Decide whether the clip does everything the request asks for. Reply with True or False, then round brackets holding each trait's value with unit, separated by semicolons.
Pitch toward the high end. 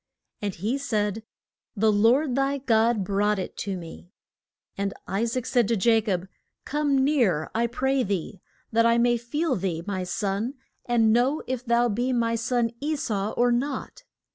True (230 Hz)